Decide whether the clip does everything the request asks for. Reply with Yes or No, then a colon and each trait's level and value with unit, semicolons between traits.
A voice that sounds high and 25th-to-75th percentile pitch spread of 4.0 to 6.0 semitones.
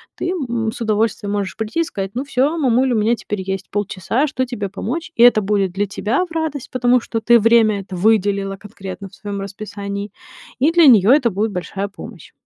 No: high, 215 Hz; average, 3.6 semitones